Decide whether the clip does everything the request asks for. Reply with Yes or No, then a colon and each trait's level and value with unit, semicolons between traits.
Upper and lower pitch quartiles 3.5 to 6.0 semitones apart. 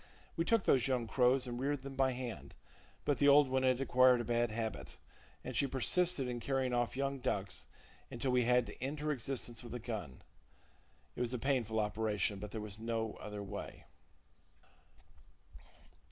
No: average, 3.0 semitones